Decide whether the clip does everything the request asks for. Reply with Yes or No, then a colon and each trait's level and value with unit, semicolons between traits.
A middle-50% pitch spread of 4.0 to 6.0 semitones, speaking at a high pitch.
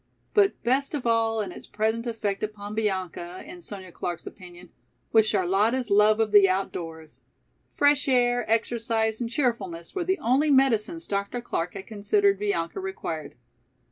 Yes: average, 4.7 semitones; high, 220 Hz